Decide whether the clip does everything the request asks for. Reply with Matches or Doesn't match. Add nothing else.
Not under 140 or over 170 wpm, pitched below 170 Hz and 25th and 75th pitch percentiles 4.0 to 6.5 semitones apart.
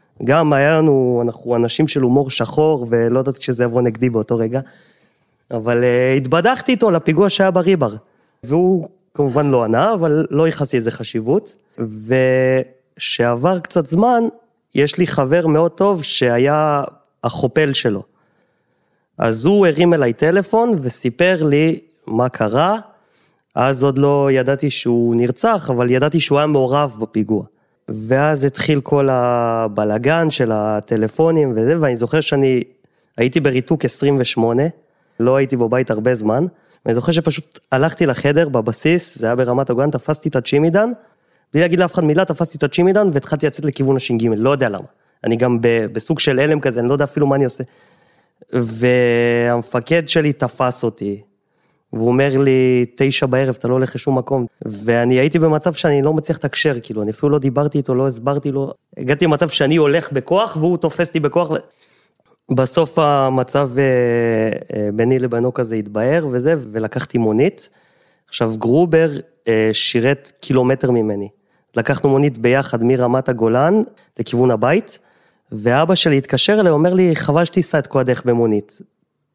Matches